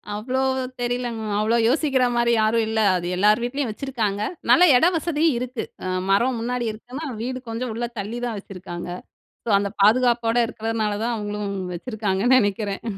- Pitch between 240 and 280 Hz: No, high, 230 Hz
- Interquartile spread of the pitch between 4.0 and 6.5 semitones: No, average, 3.1 semitones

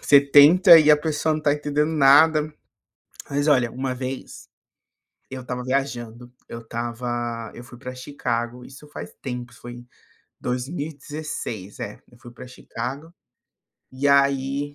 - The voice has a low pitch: Yes, low, 130 Hz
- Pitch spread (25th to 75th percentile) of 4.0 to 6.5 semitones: No, average, 3.2 semitones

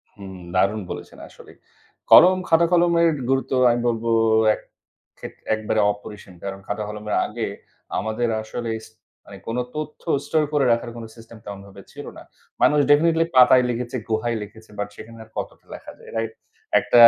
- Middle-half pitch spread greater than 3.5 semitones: Yes, average, 4.0 semitones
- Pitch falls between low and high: No, low, 115 Hz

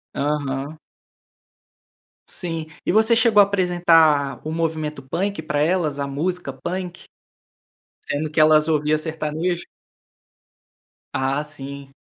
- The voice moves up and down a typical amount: Yes, average, 3.2 semitones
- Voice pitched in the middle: Yes, medium, 155 Hz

